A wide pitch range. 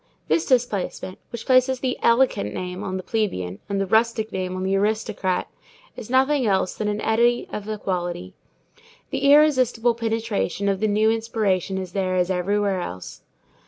No: average, 3.8 semitones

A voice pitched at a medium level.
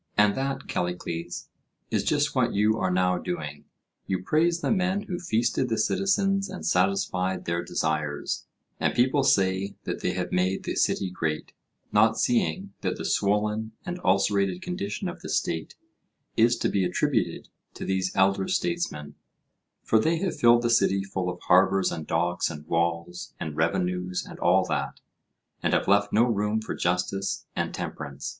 No: very low, 95 Hz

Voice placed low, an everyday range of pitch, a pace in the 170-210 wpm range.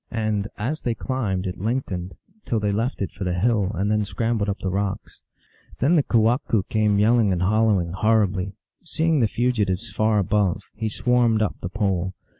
Yes: low, 105 Hz; average, 3.1 semitones; average, 185 wpm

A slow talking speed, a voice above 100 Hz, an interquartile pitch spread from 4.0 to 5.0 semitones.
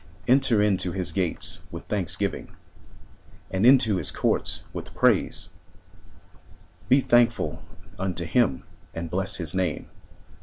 No: slow, 115 wpm; very low, 95 Hz; average, 4.6 semitones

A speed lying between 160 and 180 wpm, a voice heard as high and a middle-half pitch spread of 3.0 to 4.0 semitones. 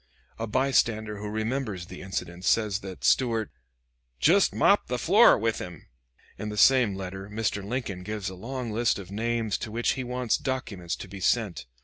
No: average, 175 wpm; low, 105 Hz; average, 3.4 semitones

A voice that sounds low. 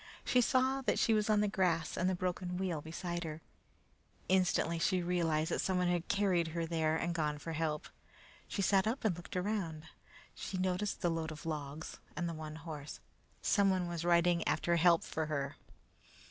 No: medium, 175 Hz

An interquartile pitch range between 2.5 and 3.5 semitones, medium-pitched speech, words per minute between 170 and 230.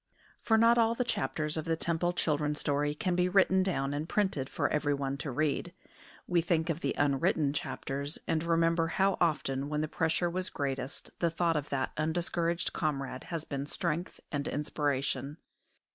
Yes: average, 3.2 semitones; medium, 155 Hz; average, 175 wpm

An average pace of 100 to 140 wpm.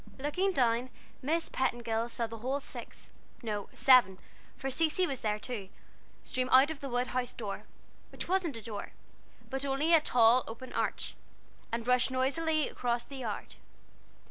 No: average, 160 wpm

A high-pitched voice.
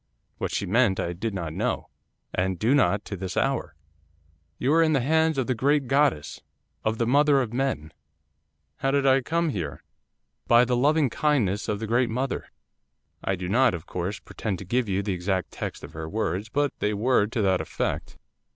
No: low, 115 Hz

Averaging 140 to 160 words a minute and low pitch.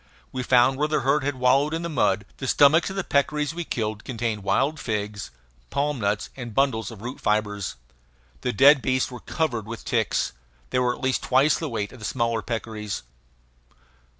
No: average, 190 wpm; low, 125 Hz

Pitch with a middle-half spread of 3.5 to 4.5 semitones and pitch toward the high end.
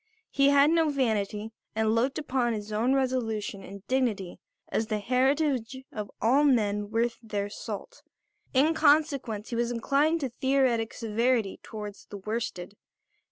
Yes: average, 4.1 semitones; high, 235 Hz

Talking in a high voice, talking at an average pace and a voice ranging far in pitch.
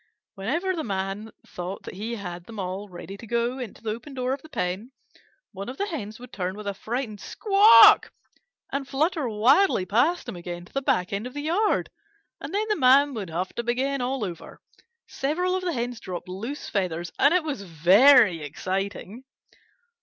Yes: high, 230 Hz; average, 190 wpm; wide, 6.4 semitones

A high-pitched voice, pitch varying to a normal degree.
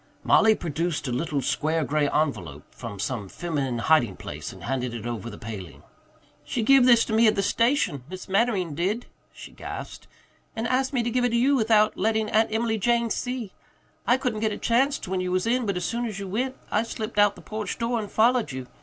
No: high, 210 Hz; wide, 7.6 semitones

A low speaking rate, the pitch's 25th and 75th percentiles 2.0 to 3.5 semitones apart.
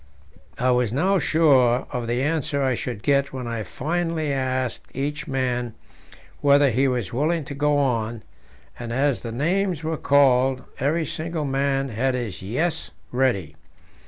No: average, 155 wpm; average, 3.2 semitones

